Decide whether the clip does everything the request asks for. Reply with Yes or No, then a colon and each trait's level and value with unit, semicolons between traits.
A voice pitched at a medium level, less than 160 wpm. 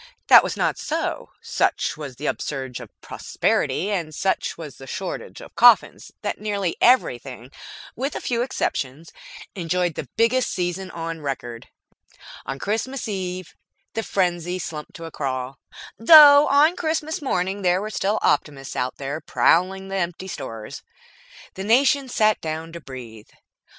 Yes: medium, 180 Hz; average, 145 wpm